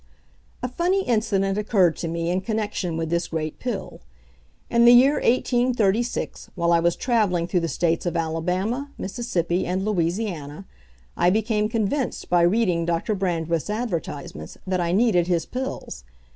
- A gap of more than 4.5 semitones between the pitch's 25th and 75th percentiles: Yes, average, 5.0 semitones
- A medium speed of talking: Yes, average, 150 wpm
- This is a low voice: No, high, 190 Hz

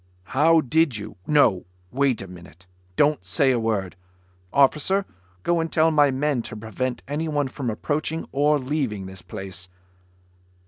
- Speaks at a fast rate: No, average, 145 wpm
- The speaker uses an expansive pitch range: Yes, wide, 6.0 semitones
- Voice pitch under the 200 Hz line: Yes, low, 135 Hz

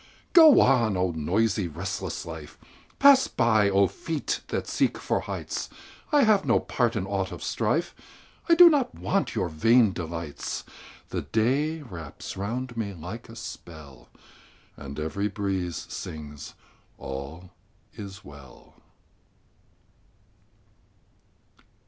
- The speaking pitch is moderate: No, low, 100 Hz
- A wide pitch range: Yes, wide, 7.4 semitones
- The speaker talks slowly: Yes, slow, 120 wpm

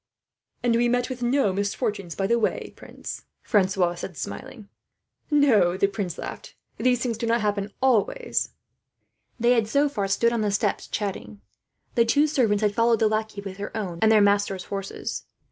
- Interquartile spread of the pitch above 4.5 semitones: No, average, 3.2 semitones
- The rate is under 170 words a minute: No, average, 180 wpm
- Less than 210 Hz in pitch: No, high, 215 Hz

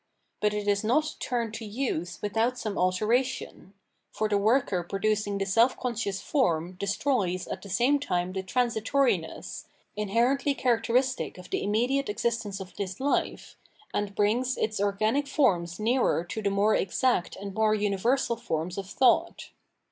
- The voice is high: Yes, high, 215 Hz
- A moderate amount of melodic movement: Yes, average, 3.9 semitones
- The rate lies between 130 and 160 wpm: Yes, average, 155 wpm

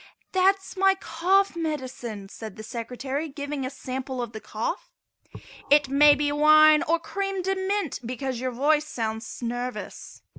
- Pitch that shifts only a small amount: No, average, 5.2 semitones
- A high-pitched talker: Yes, very high, 285 Hz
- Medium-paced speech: Yes, average, 155 wpm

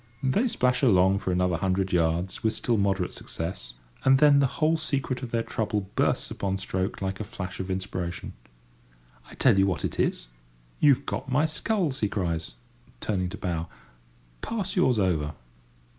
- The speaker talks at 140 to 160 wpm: No, average, 170 wpm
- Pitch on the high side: No, low, 100 Hz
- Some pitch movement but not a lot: No, wide, 6.4 semitones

